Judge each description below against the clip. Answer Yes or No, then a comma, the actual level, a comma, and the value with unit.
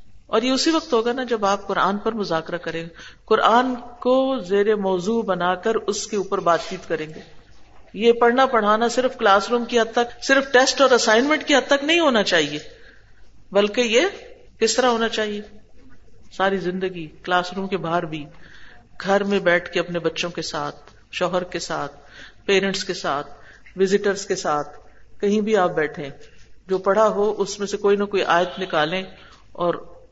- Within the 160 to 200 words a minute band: Yes, average, 180 wpm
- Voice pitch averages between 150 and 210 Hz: Yes, high, 195 Hz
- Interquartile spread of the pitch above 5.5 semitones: No, average, 5.1 semitones